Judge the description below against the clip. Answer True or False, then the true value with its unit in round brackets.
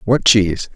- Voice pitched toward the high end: False (105 Hz)